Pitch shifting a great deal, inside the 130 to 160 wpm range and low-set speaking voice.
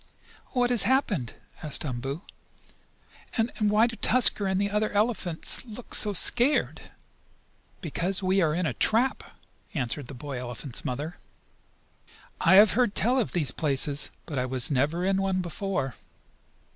No: wide, 7.0 semitones; average, 155 wpm; medium, 185 Hz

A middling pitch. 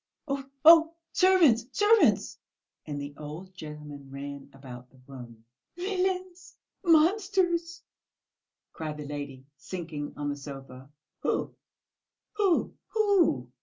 Yes: medium, 160 Hz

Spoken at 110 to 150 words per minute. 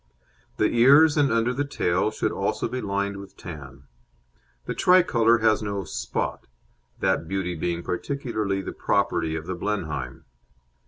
Yes: average, 145 wpm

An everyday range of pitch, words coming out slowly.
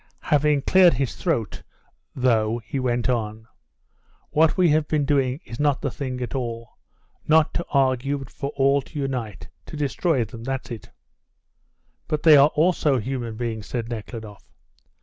No: average, 3.9 semitones; average, 160 wpm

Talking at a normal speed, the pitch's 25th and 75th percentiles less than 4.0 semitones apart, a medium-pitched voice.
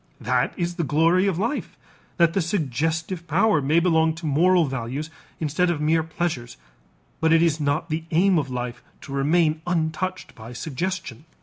Yes: average, 170 wpm; average, 2.9 semitones; medium, 160 Hz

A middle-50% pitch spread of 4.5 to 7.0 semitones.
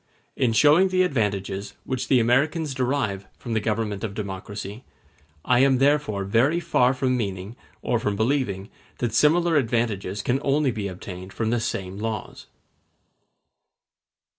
Yes: average, 5.1 semitones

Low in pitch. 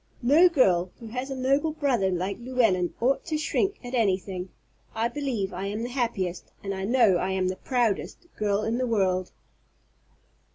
No: high, 225 Hz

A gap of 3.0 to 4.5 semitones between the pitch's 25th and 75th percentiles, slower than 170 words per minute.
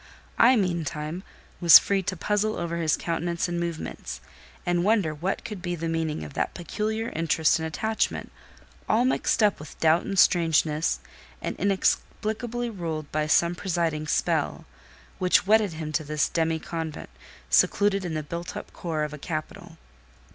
Yes: average, 3.8 semitones; average, 155 wpm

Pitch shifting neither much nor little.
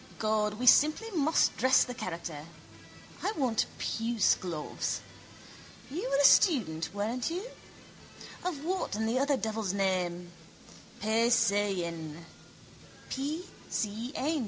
No: wide, 6.3 semitones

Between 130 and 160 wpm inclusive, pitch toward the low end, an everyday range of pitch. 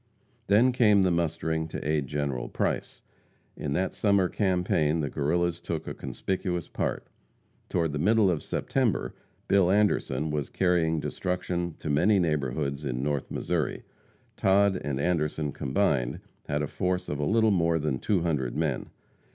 Yes: average, 150 wpm; very low, 80 Hz; average, 4.3 semitones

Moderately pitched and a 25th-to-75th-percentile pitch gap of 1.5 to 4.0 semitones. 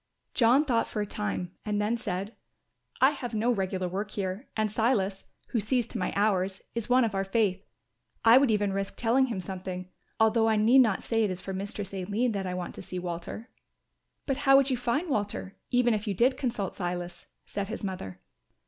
No: high, 210 Hz; average, 3.7 semitones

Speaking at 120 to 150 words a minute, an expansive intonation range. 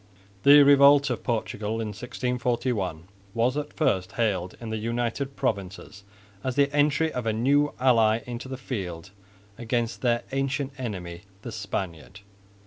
No: average, 140 wpm; average, 4.4 semitones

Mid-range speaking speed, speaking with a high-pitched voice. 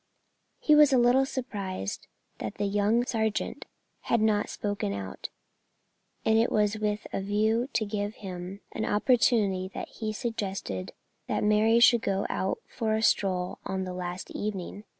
Yes: average, 160 wpm; high, 210 Hz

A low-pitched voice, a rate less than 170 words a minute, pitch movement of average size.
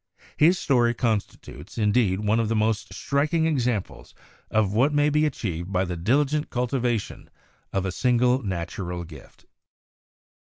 No: low, 115 Hz; average, 140 wpm; wide, 6.0 semitones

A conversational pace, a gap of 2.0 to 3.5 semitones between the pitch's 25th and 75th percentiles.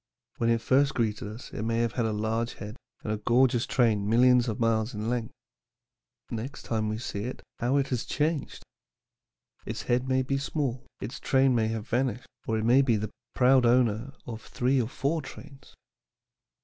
Yes: average, 190 wpm; average, 2.9 semitones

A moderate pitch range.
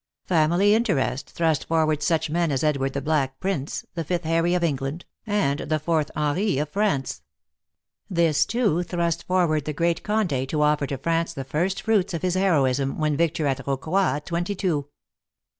Yes: average, 3.5 semitones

